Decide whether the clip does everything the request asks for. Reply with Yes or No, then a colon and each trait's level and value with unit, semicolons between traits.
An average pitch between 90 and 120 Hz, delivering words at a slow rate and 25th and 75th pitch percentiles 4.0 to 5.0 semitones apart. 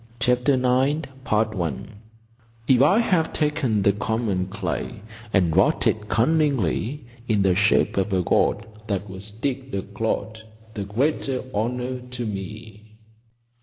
Yes: low, 110 Hz; slow, 130 wpm; average, 4.3 semitones